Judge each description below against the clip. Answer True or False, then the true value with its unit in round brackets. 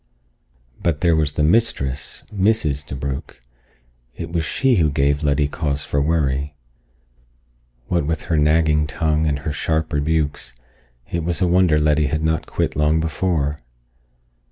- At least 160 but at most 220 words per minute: False (145 wpm)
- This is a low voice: True (75 Hz)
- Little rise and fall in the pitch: True (2.3 semitones)